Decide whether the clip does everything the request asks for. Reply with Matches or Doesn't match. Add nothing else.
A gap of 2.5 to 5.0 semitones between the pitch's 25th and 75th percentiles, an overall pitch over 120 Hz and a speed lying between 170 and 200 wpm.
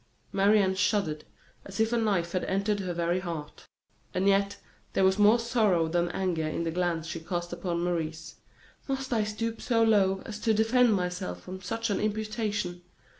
Matches